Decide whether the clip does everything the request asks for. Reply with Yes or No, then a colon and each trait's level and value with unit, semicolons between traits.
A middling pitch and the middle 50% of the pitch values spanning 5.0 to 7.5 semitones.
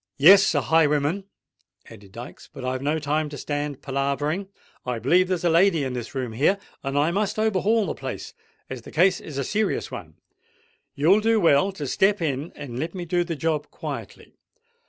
Yes: medium, 155 Hz; wide, 5.5 semitones